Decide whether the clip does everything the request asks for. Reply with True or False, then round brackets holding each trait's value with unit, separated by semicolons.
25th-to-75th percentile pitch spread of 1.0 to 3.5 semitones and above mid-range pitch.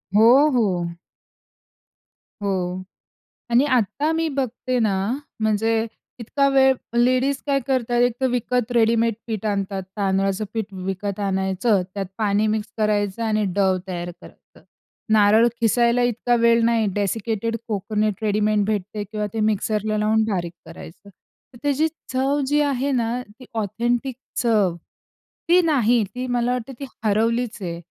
True (3.2 semitones; 220 Hz)